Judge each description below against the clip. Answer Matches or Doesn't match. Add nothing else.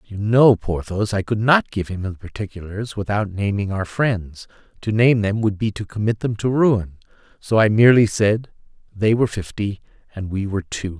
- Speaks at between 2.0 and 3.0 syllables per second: Doesn't match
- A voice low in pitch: Matches